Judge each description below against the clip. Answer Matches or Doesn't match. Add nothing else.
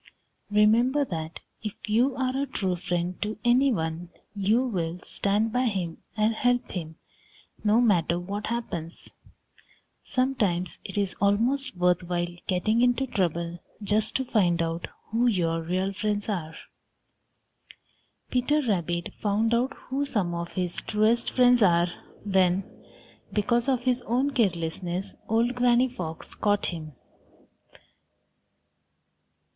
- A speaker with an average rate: Doesn't match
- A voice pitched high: Matches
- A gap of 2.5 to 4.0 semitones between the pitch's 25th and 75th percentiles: Doesn't match